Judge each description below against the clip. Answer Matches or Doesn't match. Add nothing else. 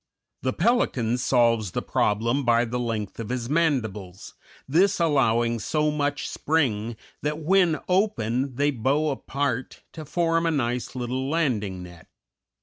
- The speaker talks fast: Doesn't match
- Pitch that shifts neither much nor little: Matches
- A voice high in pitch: Doesn't match